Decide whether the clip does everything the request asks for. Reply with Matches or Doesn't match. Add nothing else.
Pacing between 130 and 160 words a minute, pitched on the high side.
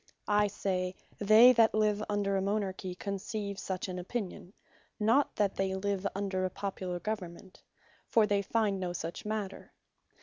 Matches